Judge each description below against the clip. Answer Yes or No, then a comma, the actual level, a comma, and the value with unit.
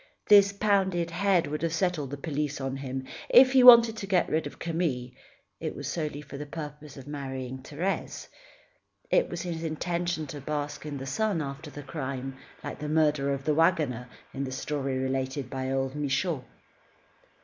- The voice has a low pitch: No, medium, 150 Hz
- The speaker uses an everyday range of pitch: Yes, average, 4.1 semitones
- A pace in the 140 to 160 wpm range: No, average, 180 wpm